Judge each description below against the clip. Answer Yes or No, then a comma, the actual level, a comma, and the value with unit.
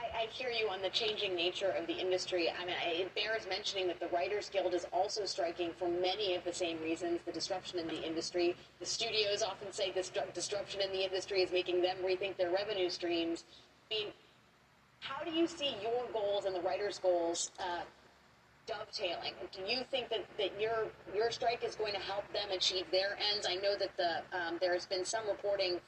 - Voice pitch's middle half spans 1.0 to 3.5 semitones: Yes, average, 2.9 semitones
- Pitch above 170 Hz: Yes, high, 190 Hz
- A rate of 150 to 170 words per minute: No, fast, 205 wpm